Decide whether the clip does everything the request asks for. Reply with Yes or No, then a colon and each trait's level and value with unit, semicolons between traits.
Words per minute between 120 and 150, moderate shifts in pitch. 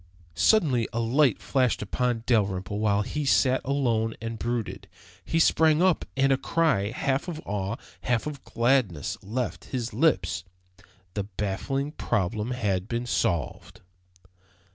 Yes: slow, 135 wpm; average, 4.7 semitones